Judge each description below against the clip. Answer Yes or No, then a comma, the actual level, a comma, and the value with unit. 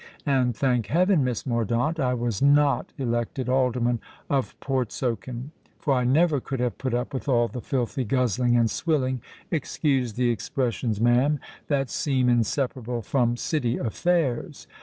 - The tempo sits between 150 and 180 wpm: No, average, 140 wpm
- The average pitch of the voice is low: Yes, low, 125 Hz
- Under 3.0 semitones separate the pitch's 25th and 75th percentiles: Yes, narrow, 2.5 semitones